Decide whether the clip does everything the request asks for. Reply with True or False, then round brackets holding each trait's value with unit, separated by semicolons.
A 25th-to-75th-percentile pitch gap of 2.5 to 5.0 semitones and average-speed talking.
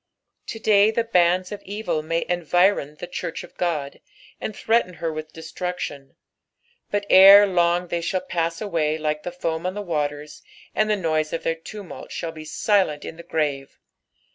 True (3.7 semitones; 175 wpm)